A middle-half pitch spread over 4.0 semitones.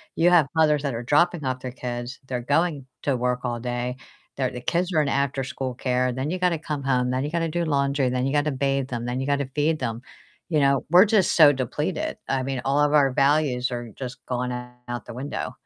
No: average, 3.1 semitones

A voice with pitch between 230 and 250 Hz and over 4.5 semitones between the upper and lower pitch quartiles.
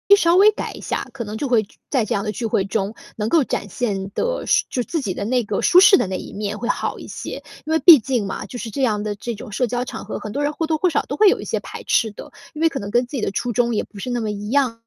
Yes: high, 235 Hz; average, 5.3 semitones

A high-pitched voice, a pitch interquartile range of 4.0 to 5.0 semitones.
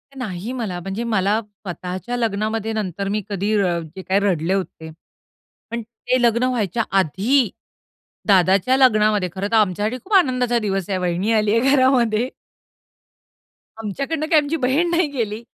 Yes: high, 215 Hz; average, 4.3 semitones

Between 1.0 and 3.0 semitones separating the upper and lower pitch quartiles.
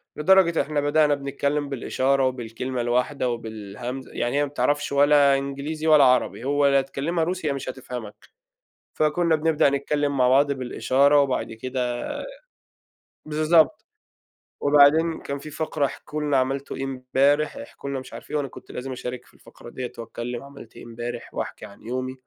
Yes: narrow, 2.5 semitones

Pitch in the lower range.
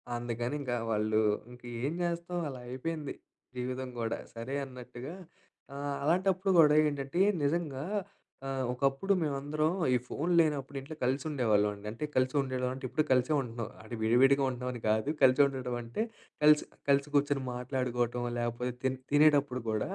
Yes: low, 130 Hz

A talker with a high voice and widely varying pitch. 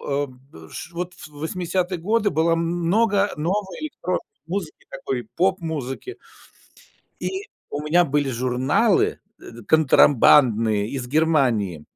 No: medium, 160 Hz; wide, 5.8 semitones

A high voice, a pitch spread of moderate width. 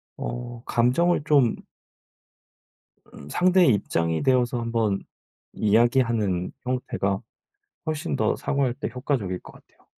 No: low, 120 Hz; average, 4.4 semitones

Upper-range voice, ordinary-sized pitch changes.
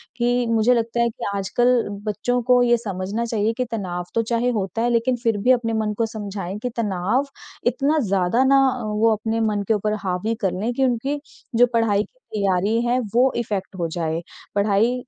Yes: high, 225 Hz; average, 3.1 semitones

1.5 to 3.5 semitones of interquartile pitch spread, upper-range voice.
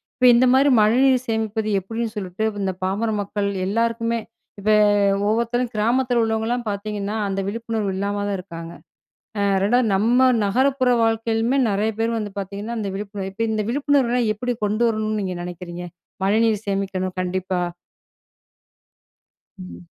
Yes: average, 2.9 semitones; high, 215 Hz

